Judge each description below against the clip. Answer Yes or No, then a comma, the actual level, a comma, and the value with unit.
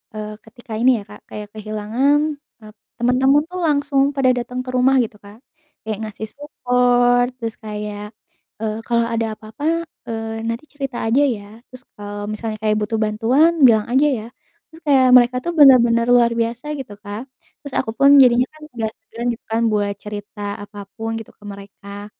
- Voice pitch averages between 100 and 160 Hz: No, high, 230 Hz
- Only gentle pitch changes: No, average, 3.0 semitones